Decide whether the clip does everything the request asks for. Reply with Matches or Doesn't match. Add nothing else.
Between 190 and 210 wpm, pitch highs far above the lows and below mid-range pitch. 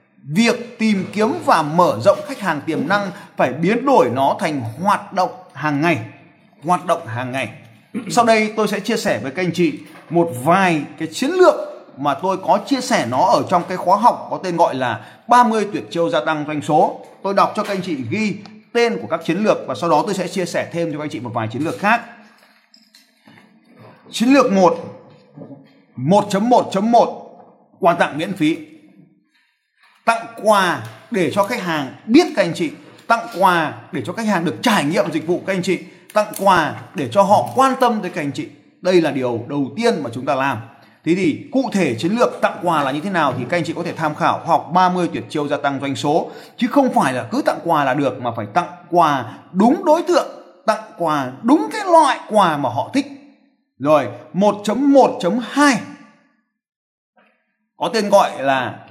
Doesn't match